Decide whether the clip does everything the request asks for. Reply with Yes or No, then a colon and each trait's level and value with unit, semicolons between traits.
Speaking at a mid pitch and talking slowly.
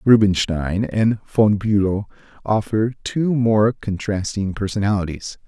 No: low, 105 Hz; slow, 100 wpm